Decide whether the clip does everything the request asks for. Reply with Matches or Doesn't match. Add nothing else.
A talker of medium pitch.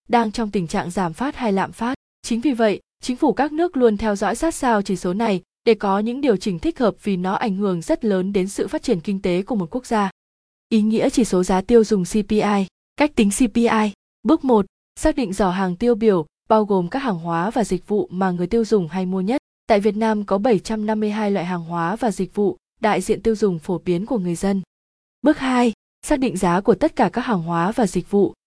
Doesn't match